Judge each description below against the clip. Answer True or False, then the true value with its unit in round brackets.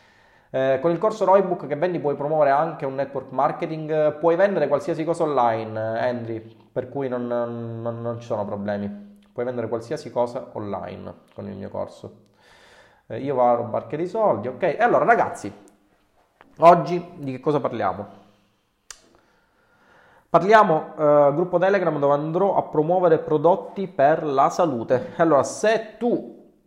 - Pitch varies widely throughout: True (6.0 semitones)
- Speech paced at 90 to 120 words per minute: False (160 wpm)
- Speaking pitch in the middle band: True (145 Hz)